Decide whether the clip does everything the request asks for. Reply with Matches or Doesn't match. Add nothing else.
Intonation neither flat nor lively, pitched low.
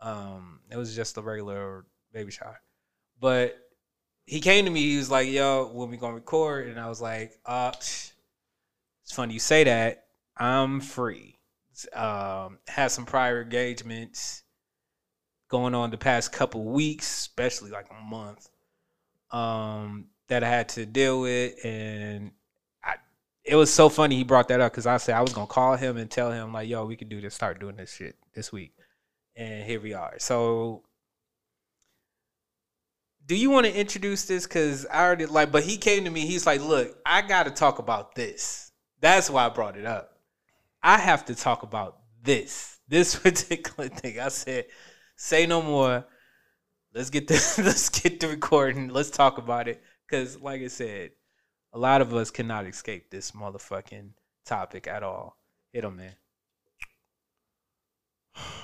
Matches